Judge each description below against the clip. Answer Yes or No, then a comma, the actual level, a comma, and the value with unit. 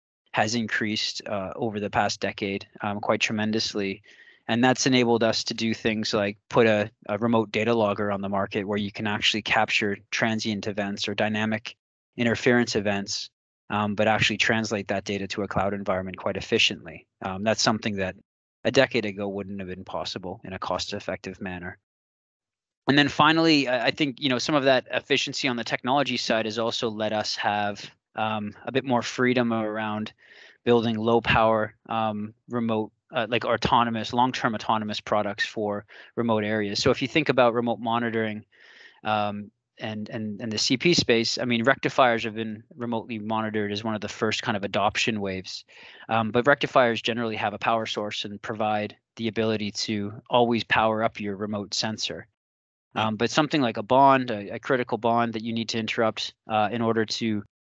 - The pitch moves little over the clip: Yes, narrow, 2.2 semitones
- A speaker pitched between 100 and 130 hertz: Yes, low, 110 Hz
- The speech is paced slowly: No, average, 180 wpm